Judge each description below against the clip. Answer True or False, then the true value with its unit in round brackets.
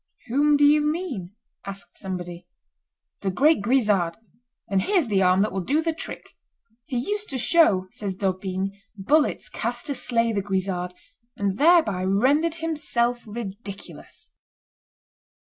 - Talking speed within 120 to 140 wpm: True (135 wpm)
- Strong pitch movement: True (7.4 semitones)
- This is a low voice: False (215 Hz)